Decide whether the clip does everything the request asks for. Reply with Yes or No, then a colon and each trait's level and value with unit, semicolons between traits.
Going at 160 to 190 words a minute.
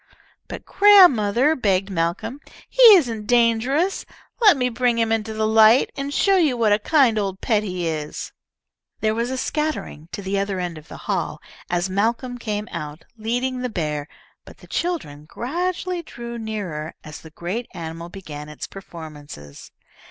Yes: average, 165 wpm